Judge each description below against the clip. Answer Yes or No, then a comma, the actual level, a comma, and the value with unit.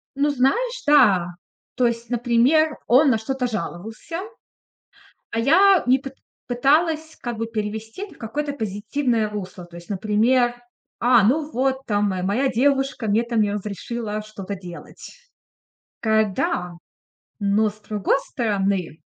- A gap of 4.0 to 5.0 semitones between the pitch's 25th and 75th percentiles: Yes, average, 4.5 semitones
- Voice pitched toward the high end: Yes, high, 230 Hz